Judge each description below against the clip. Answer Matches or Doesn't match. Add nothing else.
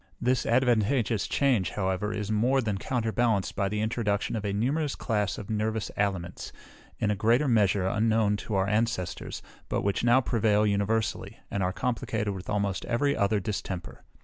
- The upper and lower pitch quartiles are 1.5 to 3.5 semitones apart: Matches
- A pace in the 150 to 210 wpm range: Matches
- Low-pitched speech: Matches